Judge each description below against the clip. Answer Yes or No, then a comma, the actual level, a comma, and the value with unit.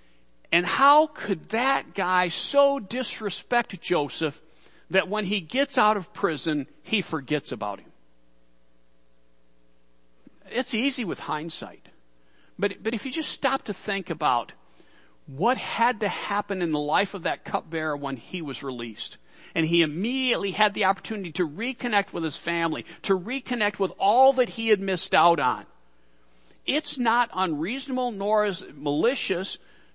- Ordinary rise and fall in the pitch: No, wide, 7.5 semitones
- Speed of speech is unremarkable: Yes, average, 150 wpm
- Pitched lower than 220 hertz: Yes, high, 190 Hz